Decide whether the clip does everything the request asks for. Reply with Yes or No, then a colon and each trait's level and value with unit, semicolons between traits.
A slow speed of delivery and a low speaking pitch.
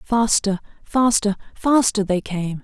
No: slow, 115 wpm; high, 210 Hz